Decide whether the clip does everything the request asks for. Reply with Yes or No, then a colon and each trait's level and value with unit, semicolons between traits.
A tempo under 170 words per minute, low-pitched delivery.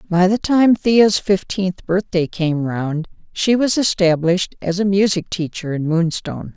No: average, 155 wpm; medium, 185 Hz